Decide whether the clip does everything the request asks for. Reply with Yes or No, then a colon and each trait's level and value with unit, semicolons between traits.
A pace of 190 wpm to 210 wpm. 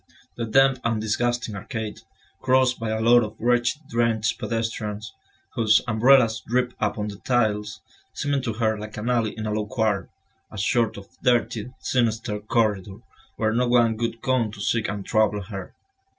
No: average, 165 wpm